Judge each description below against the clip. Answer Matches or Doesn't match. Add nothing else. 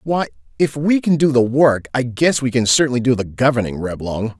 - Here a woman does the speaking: Doesn't match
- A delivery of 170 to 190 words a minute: Doesn't match